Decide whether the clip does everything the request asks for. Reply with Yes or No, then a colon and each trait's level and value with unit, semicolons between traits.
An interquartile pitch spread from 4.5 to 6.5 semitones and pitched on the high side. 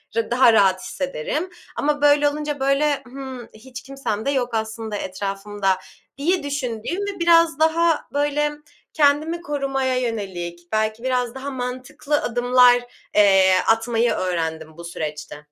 Yes: average, 5.3 semitones; very high, 250 Hz